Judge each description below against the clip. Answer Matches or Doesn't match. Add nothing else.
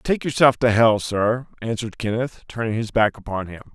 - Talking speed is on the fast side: Doesn't match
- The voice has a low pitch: Matches